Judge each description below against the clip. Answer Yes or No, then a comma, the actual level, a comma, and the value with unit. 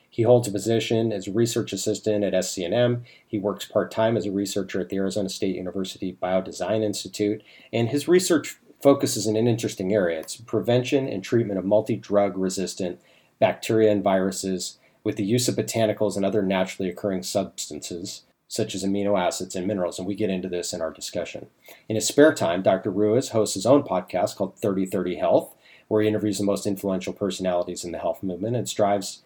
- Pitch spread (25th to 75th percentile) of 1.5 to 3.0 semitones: Yes, average, 2.7 semitones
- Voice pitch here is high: No, low, 105 Hz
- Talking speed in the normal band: Yes, average, 190 wpm